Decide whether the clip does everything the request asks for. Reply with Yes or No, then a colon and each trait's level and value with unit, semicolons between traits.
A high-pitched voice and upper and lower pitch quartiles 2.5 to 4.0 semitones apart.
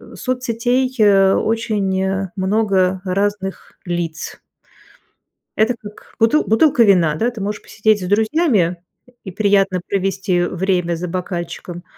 Yes: high, 195 Hz; average, 3.2 semitones